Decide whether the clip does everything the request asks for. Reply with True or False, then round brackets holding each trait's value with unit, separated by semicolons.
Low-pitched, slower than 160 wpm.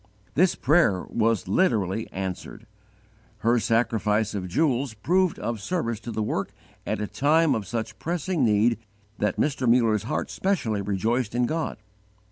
True (115 Hz; 145 wpm)